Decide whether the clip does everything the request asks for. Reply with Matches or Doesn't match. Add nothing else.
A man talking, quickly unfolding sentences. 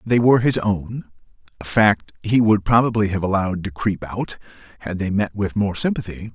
Doesn't match